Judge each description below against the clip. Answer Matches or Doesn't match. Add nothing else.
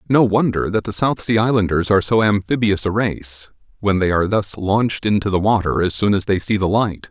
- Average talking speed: Doesn't match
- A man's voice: Matches